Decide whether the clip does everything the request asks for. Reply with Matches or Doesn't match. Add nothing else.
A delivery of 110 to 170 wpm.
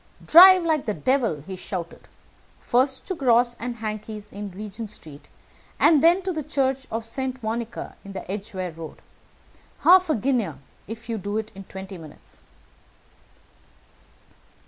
Matches